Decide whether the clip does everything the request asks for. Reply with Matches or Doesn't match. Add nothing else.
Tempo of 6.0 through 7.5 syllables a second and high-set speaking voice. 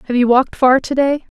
Matches